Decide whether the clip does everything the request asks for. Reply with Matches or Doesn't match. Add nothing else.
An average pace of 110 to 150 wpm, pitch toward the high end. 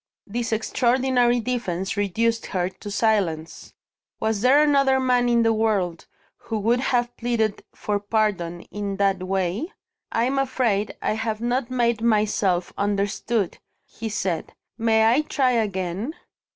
Matches